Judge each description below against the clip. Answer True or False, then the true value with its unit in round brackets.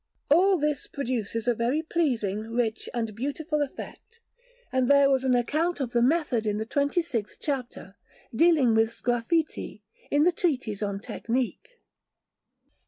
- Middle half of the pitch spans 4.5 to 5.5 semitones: True (4.9 semitones)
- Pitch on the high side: True (255 Hz)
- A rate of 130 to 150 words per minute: True (145 wpm)